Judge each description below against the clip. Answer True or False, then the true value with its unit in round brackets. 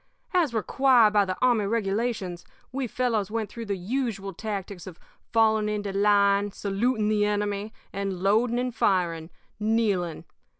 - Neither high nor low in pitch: False (210 Hz)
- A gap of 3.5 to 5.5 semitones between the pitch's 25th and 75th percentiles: False (2.7 semitones)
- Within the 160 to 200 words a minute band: False (140 wpm)